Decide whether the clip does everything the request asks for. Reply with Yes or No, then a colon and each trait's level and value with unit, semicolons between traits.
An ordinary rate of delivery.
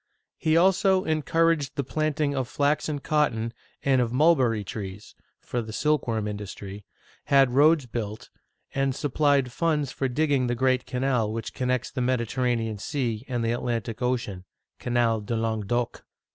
Yes: average, 155 wpm